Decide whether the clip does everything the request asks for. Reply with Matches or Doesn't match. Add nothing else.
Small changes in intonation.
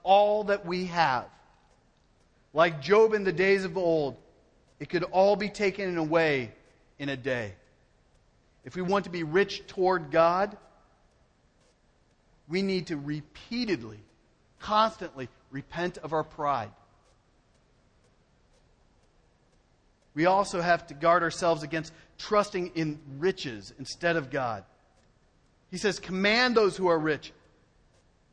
Doesn't match